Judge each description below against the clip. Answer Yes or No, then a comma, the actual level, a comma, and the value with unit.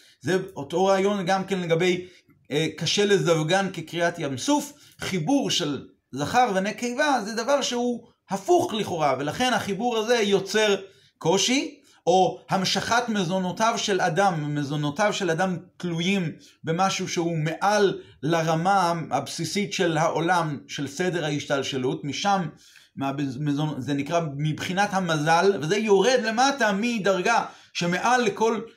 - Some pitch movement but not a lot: Yes, average, 4.4 semitones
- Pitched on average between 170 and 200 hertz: Yes, high, 190 Hz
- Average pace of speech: Yes, average, 120 wpm